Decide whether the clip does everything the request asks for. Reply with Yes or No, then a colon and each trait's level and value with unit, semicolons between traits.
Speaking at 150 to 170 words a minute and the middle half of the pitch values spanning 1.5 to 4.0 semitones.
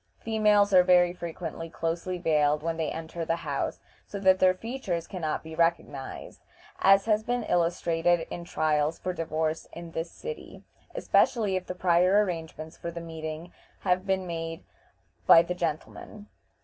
Yes: average, 160 wpm; narrow, 2.4 semitones